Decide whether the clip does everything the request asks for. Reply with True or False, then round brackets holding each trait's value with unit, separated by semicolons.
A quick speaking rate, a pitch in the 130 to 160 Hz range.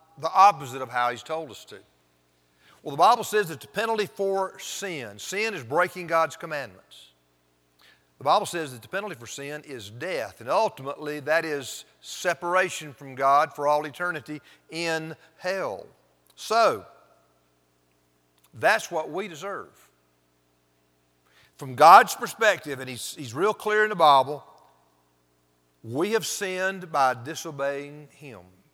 False (140 wpm; 140 Hz)